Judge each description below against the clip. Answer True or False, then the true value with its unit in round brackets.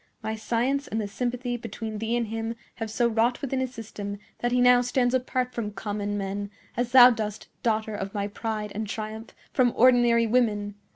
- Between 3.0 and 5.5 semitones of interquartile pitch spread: False (2.6 semitones)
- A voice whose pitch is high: True (225 Hz)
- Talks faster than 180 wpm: True (190 wpm)